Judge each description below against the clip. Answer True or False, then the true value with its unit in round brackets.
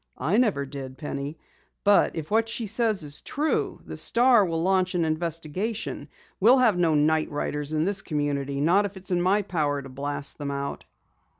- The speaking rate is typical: True (185 wpm)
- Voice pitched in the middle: True (165 Hz)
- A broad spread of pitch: True (5.8 semitones)